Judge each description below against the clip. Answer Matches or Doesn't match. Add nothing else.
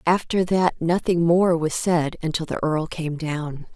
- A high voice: Doesn't match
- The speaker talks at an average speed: Matches